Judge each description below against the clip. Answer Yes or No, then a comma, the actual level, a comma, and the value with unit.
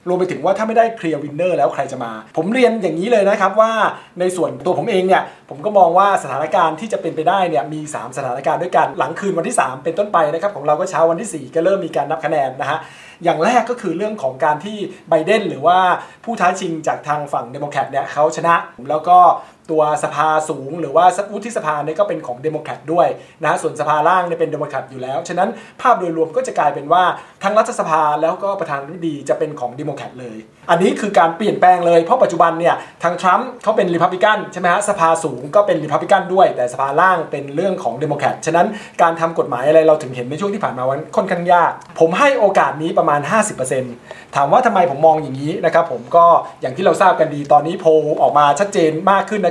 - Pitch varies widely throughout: No, average, 4.4 semitones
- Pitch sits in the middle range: Yes, medium, 170 Hz